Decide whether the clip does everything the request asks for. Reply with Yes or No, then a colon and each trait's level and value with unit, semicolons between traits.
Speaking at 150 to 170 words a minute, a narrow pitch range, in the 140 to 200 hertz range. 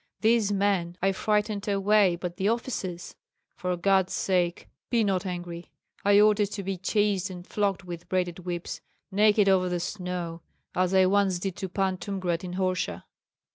Yes: average, 165 wpm; narrow, 2.3 semitones; high, 190 Hz